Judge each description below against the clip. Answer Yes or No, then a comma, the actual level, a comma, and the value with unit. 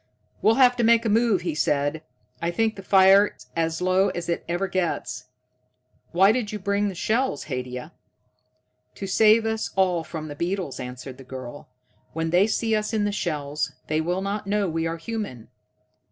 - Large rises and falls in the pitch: No, average, 5.0 semitones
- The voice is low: No, medium, 185 Hz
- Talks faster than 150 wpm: Yes, average, 180 wpm